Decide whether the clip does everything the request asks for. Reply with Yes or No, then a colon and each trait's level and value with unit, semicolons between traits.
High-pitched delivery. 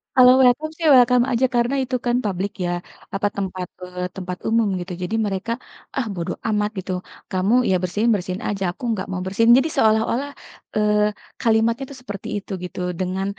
Yes: high, 210 Hz